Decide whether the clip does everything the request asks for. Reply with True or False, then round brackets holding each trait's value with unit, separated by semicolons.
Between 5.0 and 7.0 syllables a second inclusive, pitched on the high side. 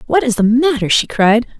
True (5.2 syllables/s; 235 Hz)